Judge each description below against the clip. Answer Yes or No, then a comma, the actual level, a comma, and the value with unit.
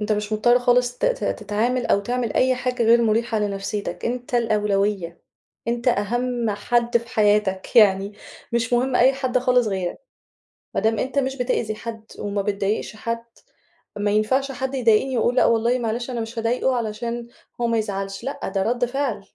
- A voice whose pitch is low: No, high, 230 Hz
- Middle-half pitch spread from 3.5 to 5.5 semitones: No, average, 2.8 semitones